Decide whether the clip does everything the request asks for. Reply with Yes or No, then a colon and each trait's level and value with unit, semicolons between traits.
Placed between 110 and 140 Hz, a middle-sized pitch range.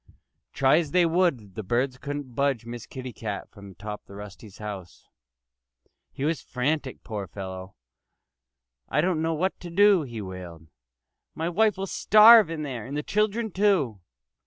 No: low, 135 Hz; wide, 8.5 semitones